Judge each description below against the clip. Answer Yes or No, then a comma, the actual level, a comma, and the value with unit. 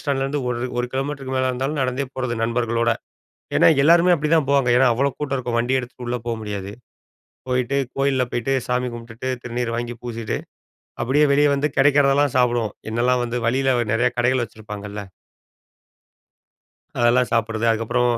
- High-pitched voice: No, low, 125 Hz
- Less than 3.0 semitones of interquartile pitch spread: Yes, narrow, 2.5 semitones